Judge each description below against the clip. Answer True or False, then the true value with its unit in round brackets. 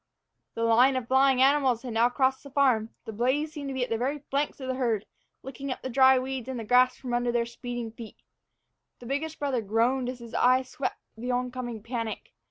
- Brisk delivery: True (215 wpm)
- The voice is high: True (255 Hz)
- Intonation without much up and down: True (2.2 semitones)